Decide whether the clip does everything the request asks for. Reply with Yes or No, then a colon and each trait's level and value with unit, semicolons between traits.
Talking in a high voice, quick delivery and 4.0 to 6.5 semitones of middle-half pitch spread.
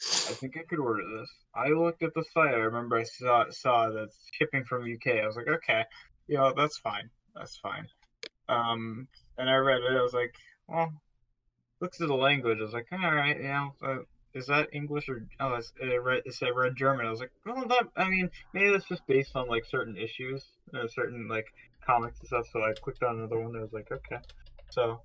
No: low, 130 Hz; fast, 235 wpm; average, 4.5 semitones